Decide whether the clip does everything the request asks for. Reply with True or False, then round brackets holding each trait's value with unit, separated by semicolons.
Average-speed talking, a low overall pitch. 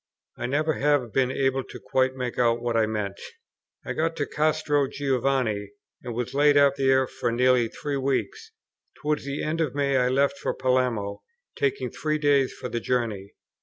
True (180 wpm; 130 Hz)